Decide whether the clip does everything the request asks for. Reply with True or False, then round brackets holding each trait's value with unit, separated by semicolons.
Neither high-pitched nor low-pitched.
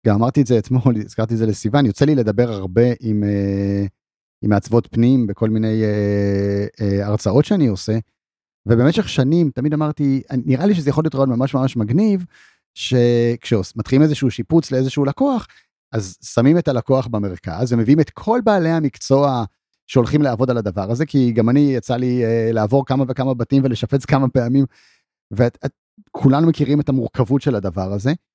False (125 Hz)